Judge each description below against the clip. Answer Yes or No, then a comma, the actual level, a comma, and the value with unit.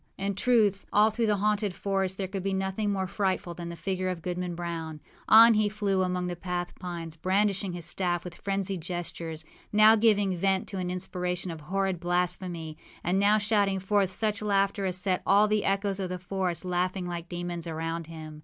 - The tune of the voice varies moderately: No, narrow, 2.2 semitones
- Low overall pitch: No, medium, 185 Hz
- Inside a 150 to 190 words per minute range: No, average, 200 wpm